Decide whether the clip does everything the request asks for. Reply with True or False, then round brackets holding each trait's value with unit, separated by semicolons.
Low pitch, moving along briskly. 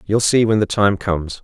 True (100 Hz; 250 wpm)